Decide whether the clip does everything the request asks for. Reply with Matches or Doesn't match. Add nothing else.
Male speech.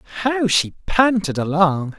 Matches